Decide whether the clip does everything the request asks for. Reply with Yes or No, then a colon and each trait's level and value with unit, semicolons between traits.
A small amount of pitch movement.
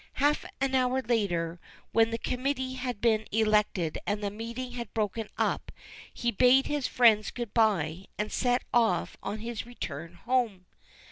No: average, 3.3 semitones